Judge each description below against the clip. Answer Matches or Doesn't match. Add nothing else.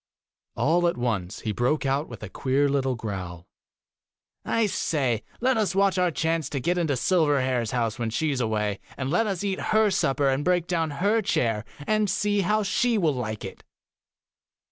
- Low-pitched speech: Doesn't match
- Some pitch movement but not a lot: Doesn't match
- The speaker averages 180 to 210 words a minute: Matches